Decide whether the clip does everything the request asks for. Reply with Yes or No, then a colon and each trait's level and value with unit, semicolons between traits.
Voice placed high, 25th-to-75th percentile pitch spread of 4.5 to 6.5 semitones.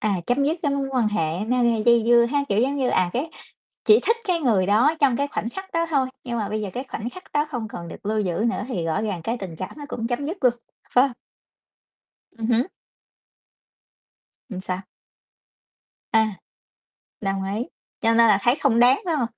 Yes: high, 235 Hz; average, 4.8 semitones